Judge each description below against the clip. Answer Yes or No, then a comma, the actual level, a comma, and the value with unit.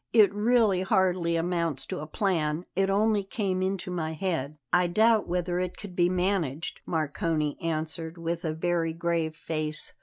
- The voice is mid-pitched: Yes, medium, 175 Hz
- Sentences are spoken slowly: No, average, 160 wpm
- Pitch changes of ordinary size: Yes, average, 3.0 semitones